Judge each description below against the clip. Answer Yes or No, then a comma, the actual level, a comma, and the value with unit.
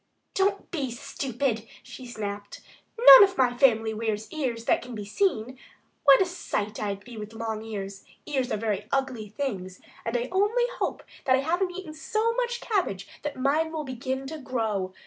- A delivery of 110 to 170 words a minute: No, average, 180 wpm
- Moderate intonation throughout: No, wide, 6.5 semitones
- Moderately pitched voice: No, very high, 255 Hz